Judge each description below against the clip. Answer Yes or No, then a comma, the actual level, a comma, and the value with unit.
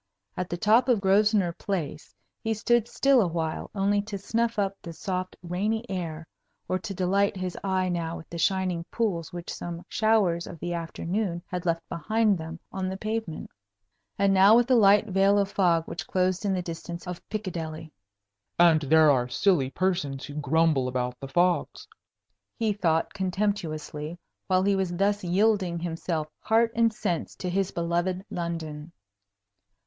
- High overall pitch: No, medium, 180 Hz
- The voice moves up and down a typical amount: Yes, average, 3.3 semitones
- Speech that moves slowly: No, average, 165 wpm